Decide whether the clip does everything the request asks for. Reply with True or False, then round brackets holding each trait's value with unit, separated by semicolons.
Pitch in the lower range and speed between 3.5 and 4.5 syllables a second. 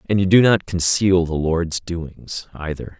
True (85 Hz; 3.9 syllables/s)